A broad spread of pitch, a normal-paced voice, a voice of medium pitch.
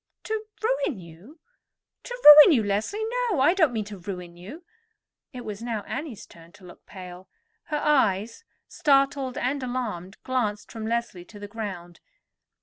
No: wide, 6.9 semitones; average, 150 wpm; high, 230 Hz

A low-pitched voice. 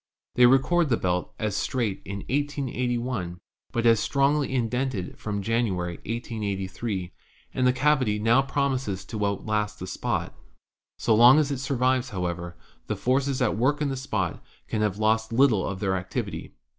Yes: low, 115 Hz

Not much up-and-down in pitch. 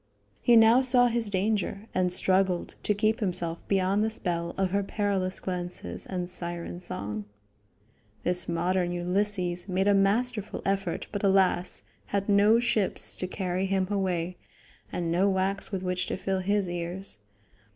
Yes: narrow, 2.3 semitones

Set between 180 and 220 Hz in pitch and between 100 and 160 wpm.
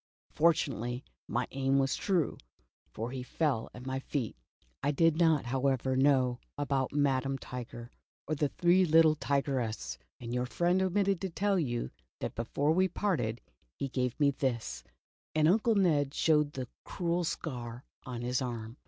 No: low, 135 Hz; average, 155 wpm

